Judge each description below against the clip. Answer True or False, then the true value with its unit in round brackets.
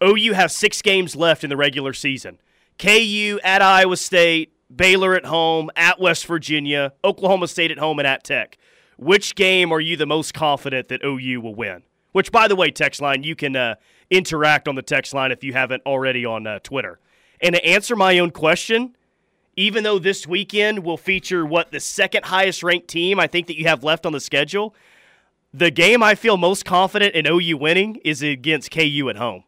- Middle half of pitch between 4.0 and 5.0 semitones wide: True (4.7 semitones)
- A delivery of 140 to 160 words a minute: False (200 wpm)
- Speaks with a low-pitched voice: False (170 Hz)